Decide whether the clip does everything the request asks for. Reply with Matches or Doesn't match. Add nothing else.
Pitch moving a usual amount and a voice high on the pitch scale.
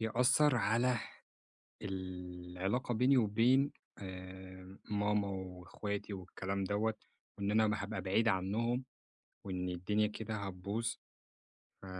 Doesn't match